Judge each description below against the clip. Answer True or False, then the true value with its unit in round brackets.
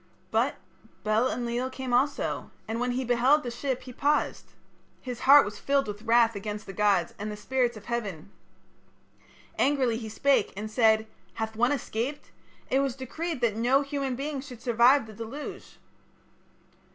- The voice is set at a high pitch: True (240 Hz)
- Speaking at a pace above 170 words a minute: False (165 wpm)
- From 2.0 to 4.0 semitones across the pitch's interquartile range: True (3.4 semitones)